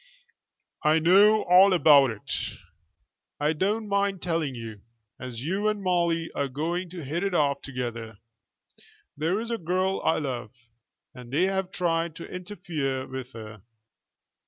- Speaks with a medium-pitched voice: Yes, medium, 165 Hz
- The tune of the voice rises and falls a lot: Yes, wide, 5.9 semitones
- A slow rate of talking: No, average, 145 wpm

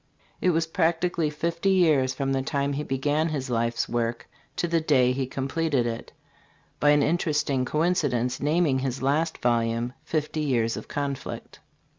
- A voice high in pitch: No, medium, 140 Hz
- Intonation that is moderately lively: Yes, average, 4.0 semitones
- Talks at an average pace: Yes, average, 155 wpm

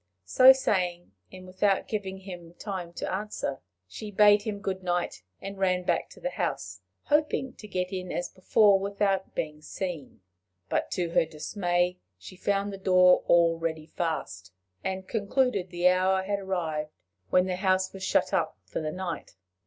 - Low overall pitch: No, medium, 185 Hz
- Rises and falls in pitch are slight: Yes, narrow, 2.3 semitones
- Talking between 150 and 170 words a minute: Yes, average, 165 wpm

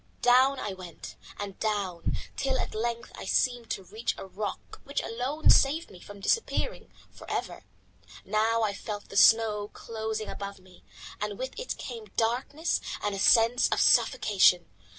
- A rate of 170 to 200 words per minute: No, average, 160 wpm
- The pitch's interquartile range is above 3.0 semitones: Yes, average, 3.5 semitones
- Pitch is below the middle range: No, high, 220 Hz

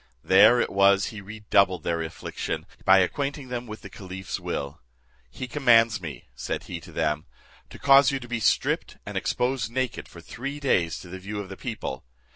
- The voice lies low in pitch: Yes, low, 105 Hz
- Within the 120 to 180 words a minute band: No, average, 190 wpm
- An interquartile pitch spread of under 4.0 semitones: No, average, 5.0 semitones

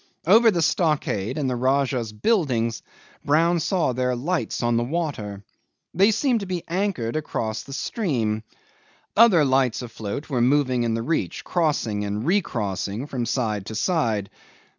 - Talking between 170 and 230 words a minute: No, average, 150 wpm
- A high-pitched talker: No, low, 130 Hz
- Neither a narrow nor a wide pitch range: No, wide, 6.8 semitones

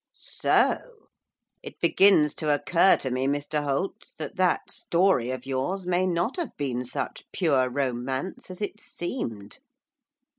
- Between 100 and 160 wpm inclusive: Yes, average, 140 wpm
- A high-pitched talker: No, medium, 150 Hz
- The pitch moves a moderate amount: No, wide, 5.9 semitones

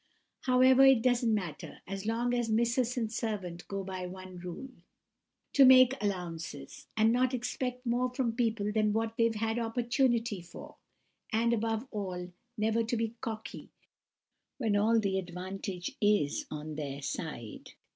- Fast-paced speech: No, average, 145 wpm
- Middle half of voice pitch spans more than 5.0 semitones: No, average, 4.2 semitones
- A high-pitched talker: Yes, high, 220 Hz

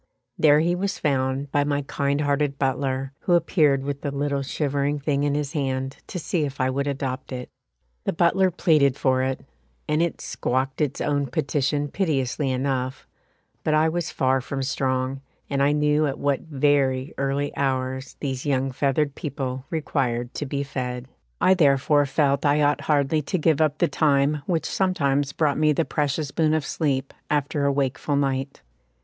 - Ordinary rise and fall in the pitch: No, narrow, 2.0 semitones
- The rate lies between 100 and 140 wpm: No, average, 175 wpm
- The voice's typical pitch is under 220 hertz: Yes, medium, 140 Hz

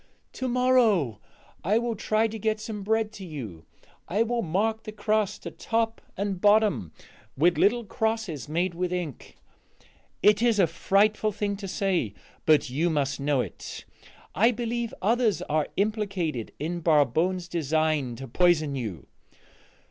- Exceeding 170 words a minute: No, average, 150 wpm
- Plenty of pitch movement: Yes, wide, 5.8 semitones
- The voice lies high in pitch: Yes, high, 195 Hz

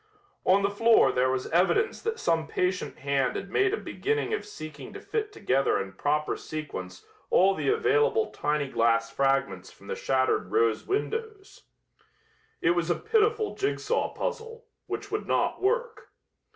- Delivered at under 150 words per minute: No, average, 155 wpm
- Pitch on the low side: No, high, 195 Hz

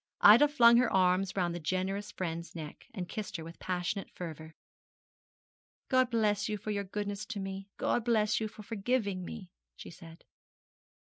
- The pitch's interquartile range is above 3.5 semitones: No, average, 3.2 semitones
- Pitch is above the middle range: Yes, high, 200 Hz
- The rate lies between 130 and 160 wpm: No, average, 170 wpm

